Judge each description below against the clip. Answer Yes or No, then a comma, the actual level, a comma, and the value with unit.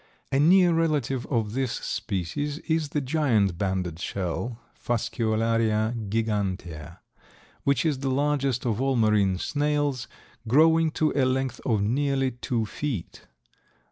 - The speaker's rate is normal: No, slow, 125 wpm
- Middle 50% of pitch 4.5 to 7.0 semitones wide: Yes, average, 5.2 semitones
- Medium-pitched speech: No, low, 125 Hz